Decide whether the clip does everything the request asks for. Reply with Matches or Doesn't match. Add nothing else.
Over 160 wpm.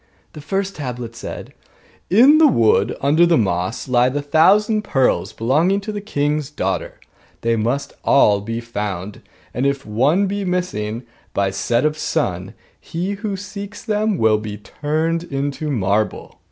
Doesn't match